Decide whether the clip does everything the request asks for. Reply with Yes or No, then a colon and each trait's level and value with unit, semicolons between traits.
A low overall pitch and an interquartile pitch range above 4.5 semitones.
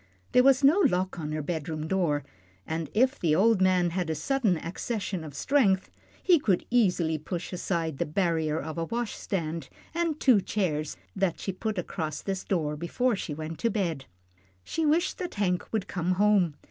No: medium, 185 Hz; wide, 5.5 semitones